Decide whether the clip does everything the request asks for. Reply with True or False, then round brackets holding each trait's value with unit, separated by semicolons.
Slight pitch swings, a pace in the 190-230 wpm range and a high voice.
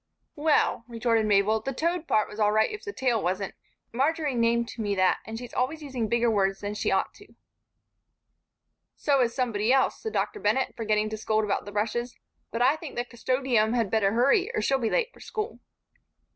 False (3.9 semitones; 200 wpm; 235 Hz)